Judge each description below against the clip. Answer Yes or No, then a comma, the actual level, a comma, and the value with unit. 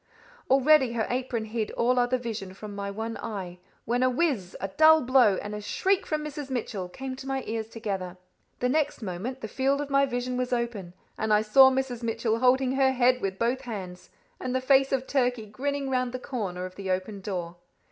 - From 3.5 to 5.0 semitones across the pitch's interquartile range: Yes, average, 4.1 semitones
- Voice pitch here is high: Yes, high, 245 Hz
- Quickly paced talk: Yes, fast, 210 wpm